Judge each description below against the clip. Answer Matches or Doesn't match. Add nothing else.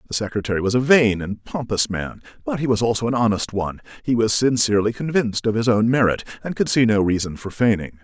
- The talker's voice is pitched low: Matches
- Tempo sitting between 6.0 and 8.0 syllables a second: Matches